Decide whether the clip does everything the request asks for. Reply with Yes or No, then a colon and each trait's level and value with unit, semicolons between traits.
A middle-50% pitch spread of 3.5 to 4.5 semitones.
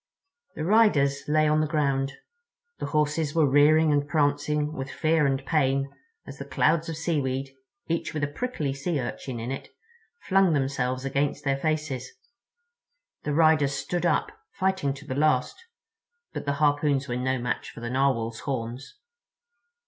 No: narrow, 2.4 semitones